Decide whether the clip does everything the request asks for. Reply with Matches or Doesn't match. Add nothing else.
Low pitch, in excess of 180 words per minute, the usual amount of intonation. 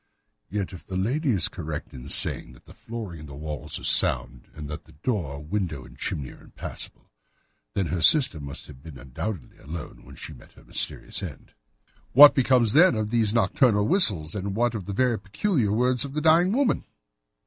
Doesn't match